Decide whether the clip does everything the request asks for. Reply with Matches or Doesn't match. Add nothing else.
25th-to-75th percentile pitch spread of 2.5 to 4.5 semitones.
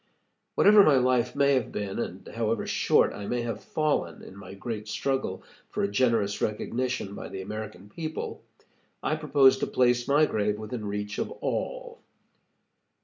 Doesn't match